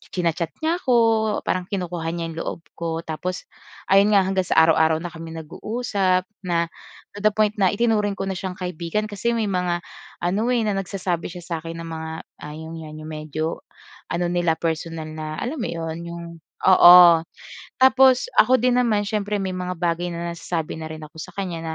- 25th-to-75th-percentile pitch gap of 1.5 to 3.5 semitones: No, average, 3.9 semitones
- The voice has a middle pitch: Yes, medium, 180 Hz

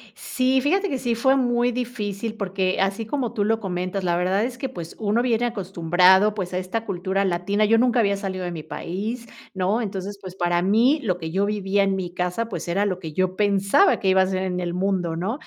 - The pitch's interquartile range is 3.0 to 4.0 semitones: Yes, average, 3.7 semitones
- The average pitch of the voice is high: Yes, high, 195 Hz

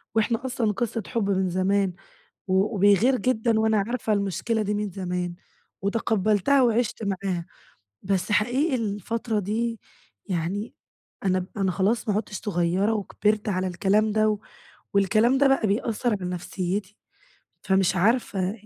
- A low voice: No, high, 205 Hz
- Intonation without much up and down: No, average, 3.1 semitones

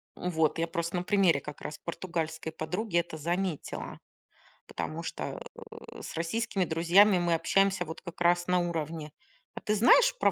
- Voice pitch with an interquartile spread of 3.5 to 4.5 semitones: No, narrow, 2.6 semitones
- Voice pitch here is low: No, medium, 170 Hz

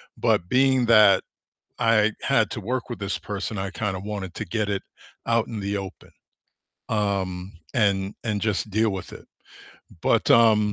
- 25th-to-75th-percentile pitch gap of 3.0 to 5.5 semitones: No, narrow, 2.4 semitones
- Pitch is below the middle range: Yes, low, 105 Hz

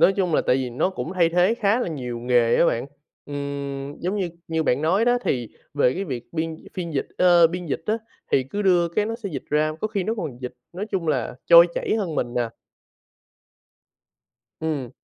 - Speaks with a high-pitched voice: No, medium, 165 Hz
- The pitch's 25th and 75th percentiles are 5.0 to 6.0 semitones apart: Yes, wide, 5.5 semitones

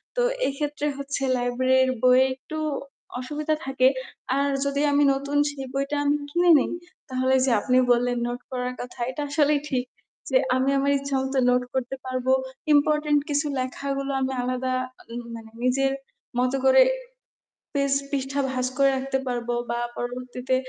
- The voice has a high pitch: Yes, very high, 265 Hz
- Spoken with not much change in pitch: Yes, narrow, 1.8 semitones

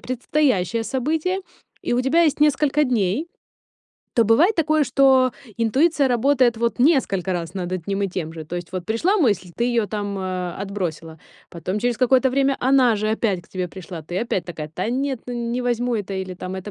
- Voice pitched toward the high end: Yes, high, 230 Hz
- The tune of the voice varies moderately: No, wide, 6.2 semitones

